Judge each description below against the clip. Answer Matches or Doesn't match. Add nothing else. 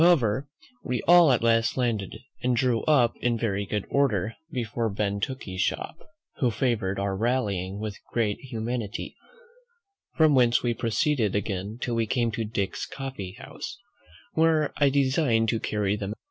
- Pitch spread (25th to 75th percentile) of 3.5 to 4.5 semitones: Matches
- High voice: Doesn't match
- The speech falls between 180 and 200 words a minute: Doesn't match